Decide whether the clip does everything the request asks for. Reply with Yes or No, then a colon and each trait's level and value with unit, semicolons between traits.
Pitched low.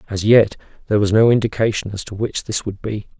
Yes: low, 105 Hz